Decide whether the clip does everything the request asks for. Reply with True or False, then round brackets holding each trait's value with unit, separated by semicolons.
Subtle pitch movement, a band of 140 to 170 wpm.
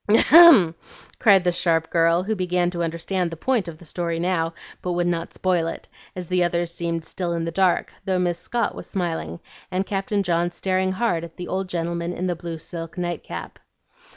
False (1.8 semitones; 200 wpm)